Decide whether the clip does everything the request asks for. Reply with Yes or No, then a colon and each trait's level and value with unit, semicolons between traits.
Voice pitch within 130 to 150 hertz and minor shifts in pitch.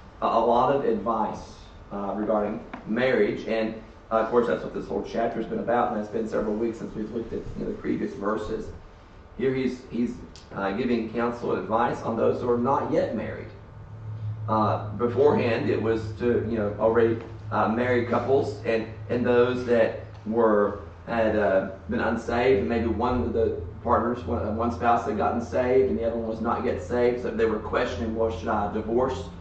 No: low, 110 Hz; narrow, 1.9 semitones